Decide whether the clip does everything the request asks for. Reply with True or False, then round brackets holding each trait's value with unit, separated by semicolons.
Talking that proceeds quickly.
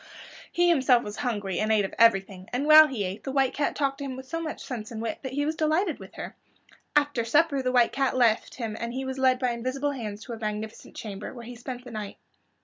True (250 wpm)